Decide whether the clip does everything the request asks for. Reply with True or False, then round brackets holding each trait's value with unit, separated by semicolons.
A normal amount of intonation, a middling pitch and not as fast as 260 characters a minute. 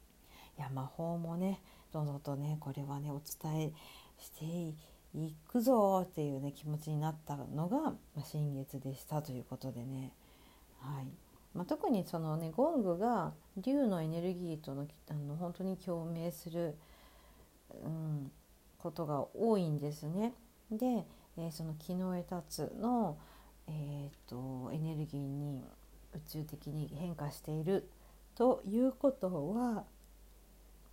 True (4.4 semitones; 155 Hz; 250 characters per minute)